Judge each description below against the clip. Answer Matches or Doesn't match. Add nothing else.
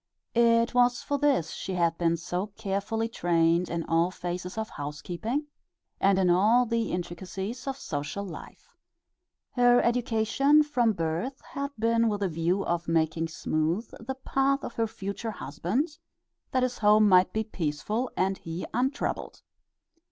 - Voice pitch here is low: Doesn't match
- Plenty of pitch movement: Matches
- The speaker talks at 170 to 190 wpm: Doesn't match